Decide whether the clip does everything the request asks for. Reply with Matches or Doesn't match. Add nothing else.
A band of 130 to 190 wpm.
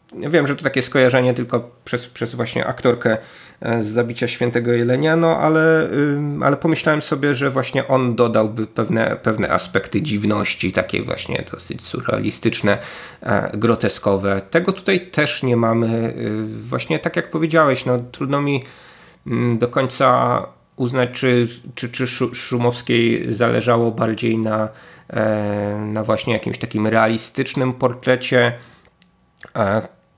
Doesn't match